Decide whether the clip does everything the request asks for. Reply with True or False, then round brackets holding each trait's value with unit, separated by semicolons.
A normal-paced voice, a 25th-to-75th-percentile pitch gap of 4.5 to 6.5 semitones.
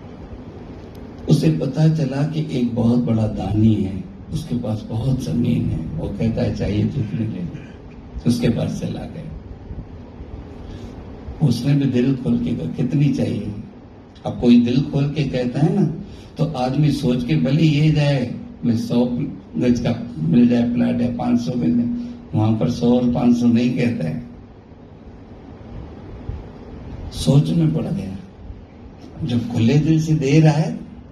True (150 wpm; 5.1 semitones)